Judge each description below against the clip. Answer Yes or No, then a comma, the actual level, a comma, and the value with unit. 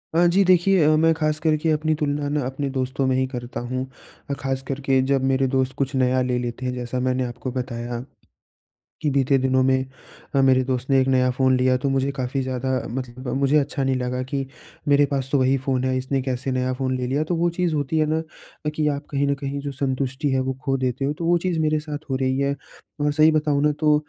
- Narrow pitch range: Yes, narrow, 2.3 semitones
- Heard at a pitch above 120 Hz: Yes, low, 135 Hz